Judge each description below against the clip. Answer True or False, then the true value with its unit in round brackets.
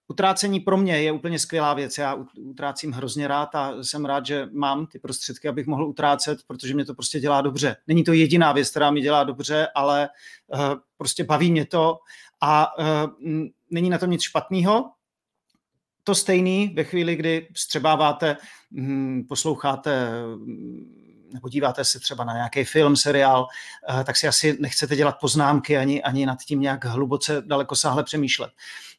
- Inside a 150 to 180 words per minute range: True (155 wpm)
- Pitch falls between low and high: True (145 Hz)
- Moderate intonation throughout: False (2.1 semitones)